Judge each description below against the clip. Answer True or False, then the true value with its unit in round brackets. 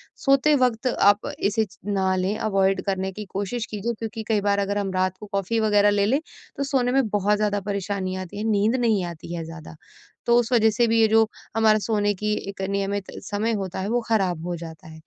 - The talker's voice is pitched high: True (205 Hz)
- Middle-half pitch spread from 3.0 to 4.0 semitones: False (2.5 semitones)